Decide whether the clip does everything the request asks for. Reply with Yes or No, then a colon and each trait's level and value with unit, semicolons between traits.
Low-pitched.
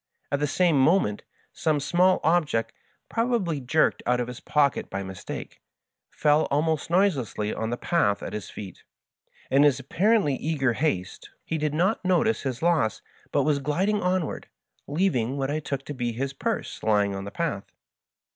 No: medium, 145 Hz